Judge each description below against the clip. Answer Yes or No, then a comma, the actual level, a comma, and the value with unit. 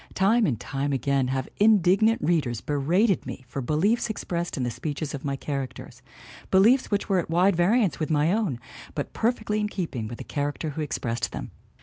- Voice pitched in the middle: Yes, medium, 160 Hz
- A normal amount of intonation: No, wide, 6.7 semitones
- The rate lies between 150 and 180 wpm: No, average, 190 wpm